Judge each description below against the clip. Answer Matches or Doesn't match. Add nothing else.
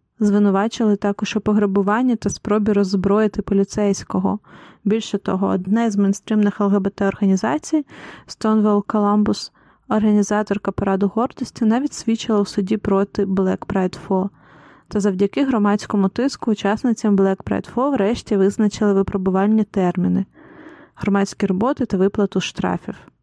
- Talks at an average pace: Matches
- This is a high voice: Matches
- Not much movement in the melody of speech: Matches